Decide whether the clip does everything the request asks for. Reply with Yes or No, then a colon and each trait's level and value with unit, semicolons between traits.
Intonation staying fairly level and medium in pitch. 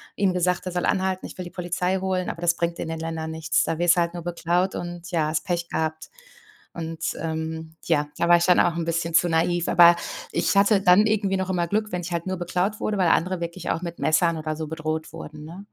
Yes: narrow, 2.0 semitones; medium, 170 Hz